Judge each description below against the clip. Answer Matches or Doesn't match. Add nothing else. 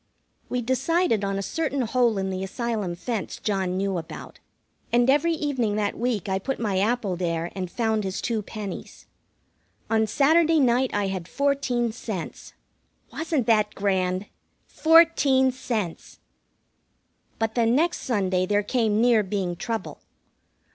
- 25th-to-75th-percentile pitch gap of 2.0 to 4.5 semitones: Doesn't match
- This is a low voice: Doesn't match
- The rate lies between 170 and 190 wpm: Doesn't match